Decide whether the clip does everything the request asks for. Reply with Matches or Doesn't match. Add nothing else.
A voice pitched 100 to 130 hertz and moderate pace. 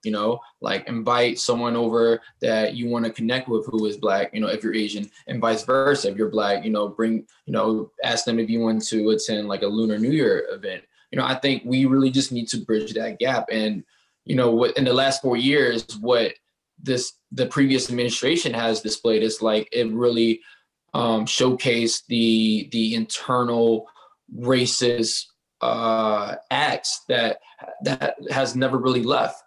Matches